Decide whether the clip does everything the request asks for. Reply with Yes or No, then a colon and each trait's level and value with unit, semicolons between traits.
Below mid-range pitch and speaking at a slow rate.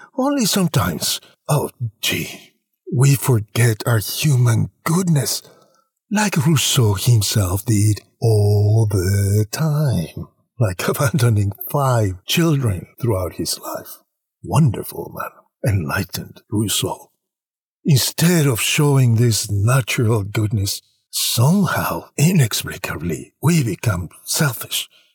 Yes: low, 120 Hz; slow, 90 wpm